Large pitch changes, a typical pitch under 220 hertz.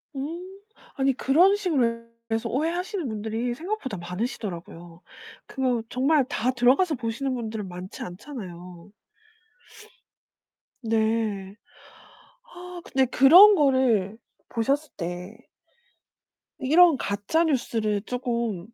No: wide, 5.9 semitones; high, 245 Hz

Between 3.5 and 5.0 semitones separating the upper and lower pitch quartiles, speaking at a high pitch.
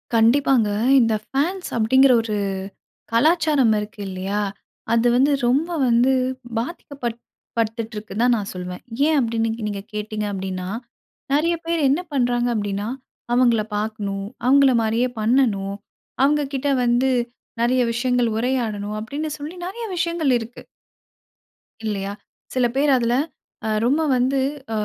Yes: average, 4.2 semitones; high, 240 Hz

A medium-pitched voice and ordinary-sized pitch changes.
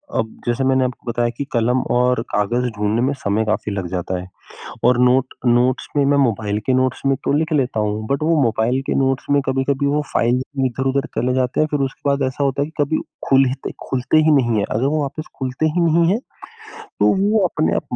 No: low, 130 Hz; average, 3.1 semitones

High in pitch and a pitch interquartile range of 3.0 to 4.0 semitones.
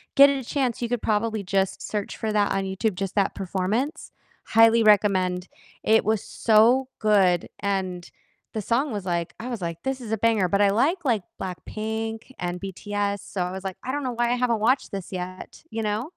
Yes: high, 210 Hz; average, 3.3 semitones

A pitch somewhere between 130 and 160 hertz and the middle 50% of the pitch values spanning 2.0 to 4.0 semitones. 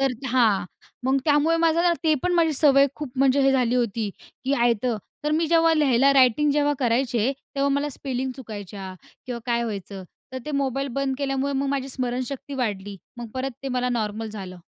No: very high, 265 Hz; average, 3.1 semitones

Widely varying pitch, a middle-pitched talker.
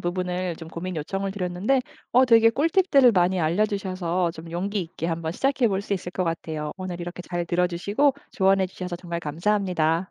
No: average, 2.9 semitones; medium, 180 Hz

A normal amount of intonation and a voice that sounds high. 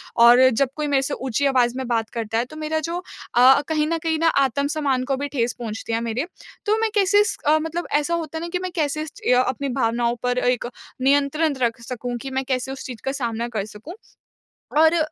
Yes: average, 4.3 semitones; very high, 270 Hz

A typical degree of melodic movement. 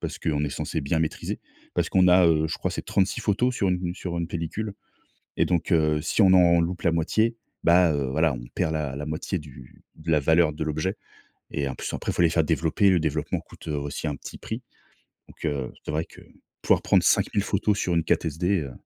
Yes: average, 3.1 semitones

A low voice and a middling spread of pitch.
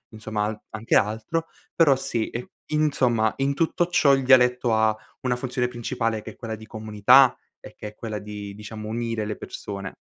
Yes: low, 115 Hz; average, 3.2 semitones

